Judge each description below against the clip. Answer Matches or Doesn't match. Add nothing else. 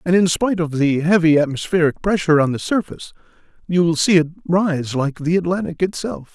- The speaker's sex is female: Doesn't match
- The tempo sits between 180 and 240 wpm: Matches